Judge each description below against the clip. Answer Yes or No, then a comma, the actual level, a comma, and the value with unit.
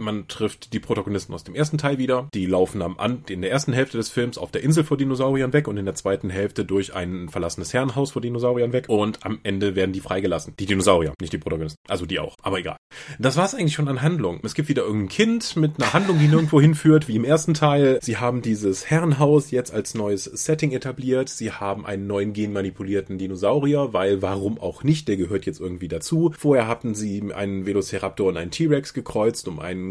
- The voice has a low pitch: Yes, low, 120 Hz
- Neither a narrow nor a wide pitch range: No, wide, 6.6 semitones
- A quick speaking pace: Yes, fast, 220 wpm